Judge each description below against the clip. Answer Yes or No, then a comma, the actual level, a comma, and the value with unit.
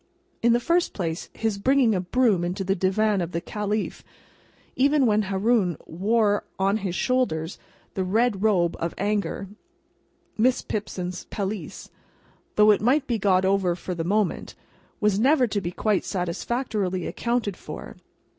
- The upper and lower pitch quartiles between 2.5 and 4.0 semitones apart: Yes, average, 3.7 semitones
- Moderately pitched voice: No, high, 205 Hz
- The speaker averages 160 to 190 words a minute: No, average, 150 wpm